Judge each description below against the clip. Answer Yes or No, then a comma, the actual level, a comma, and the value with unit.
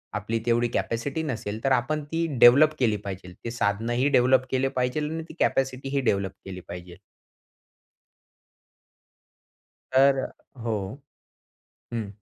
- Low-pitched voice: Yes, low, 120 Hz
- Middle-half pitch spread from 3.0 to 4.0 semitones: No, average, 4.4 semitones